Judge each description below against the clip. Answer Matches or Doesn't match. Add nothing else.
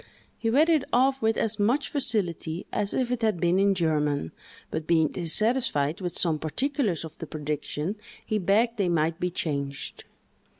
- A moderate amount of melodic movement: Doesn't match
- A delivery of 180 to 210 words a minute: Doesn't match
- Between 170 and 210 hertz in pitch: Matches